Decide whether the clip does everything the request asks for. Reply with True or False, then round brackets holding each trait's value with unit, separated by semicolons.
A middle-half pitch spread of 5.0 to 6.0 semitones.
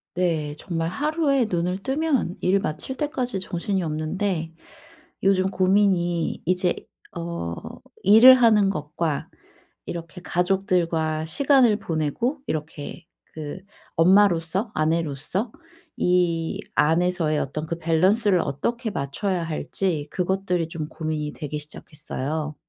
False (4.0 semitones)